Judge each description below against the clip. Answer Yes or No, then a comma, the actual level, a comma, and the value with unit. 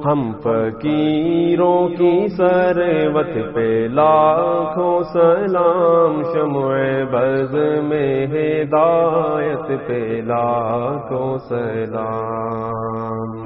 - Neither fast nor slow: No, slow, 65 wpm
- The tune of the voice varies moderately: No, wide, 5.9 semitones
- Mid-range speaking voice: Yes, medium, 150 Hz